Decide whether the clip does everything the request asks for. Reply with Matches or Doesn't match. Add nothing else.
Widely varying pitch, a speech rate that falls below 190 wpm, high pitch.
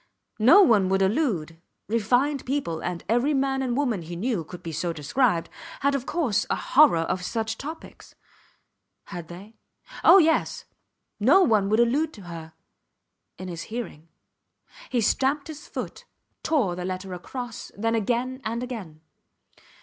Matches